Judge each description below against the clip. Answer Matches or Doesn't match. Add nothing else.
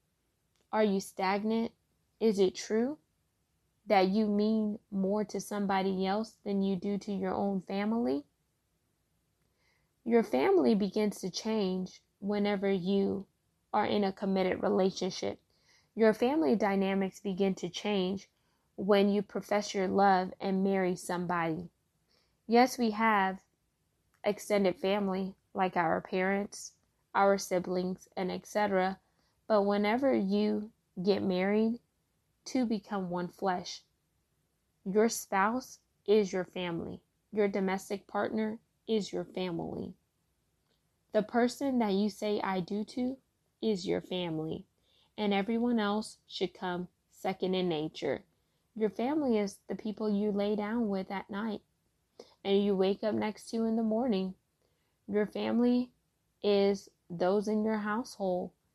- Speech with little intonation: Matches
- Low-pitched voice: Doesn't match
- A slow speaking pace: Matches